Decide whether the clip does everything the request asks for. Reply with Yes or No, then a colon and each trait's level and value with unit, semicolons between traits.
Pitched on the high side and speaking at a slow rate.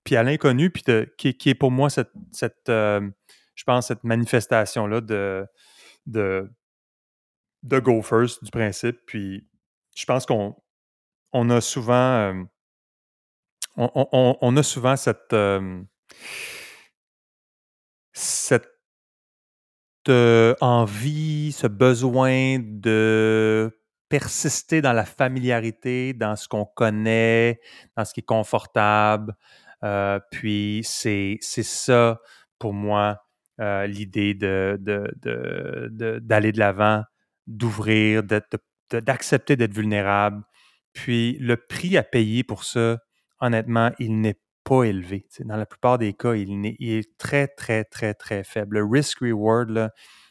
No: low, 115 Hz; slow, 135 wpm